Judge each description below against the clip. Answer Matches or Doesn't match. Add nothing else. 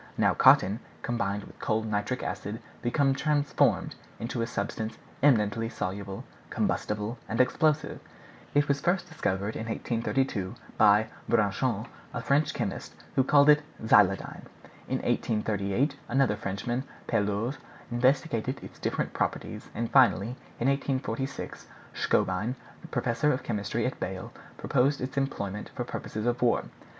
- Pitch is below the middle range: Matches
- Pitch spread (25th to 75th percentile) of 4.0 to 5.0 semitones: Matches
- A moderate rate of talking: Doesn't match